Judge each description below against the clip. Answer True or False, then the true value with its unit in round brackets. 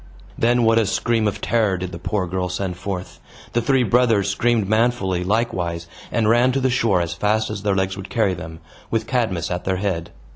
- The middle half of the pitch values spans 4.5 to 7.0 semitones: False (4.0 semitones)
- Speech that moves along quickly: True (210 wpm)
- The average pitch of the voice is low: True (100 Hz)